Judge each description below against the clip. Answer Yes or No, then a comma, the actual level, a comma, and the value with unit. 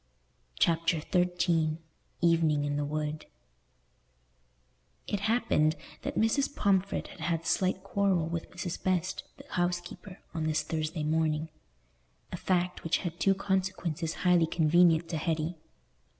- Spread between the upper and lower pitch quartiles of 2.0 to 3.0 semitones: Yes, narrow, 2.6 semitones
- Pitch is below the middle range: No, medium, 170 Hz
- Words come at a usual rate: No, slow, 125 wpm